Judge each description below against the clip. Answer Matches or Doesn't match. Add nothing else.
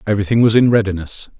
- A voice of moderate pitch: Doesn't match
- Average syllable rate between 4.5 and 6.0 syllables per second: Doesn't match